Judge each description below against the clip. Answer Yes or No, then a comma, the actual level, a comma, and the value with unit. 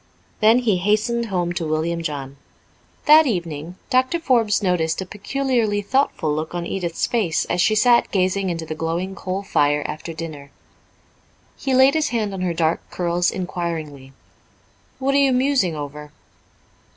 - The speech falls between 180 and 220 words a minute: No, average, 155 wpm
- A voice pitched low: No, medium, 185 Hz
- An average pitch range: No, wide, 6.1 semitones